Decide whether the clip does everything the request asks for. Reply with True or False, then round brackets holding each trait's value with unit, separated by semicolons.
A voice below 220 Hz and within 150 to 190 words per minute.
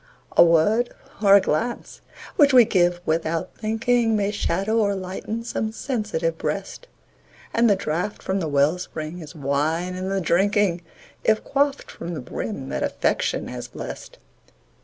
True (190 Hz; 155 wpm)